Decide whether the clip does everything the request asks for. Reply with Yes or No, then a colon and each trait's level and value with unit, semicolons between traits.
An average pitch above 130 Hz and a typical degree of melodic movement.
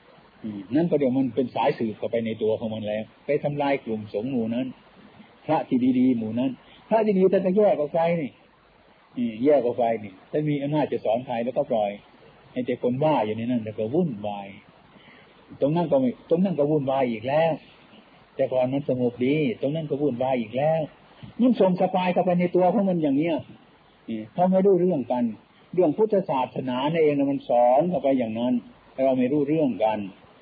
No: medium, 140 Hz; wide, 6.8 semitones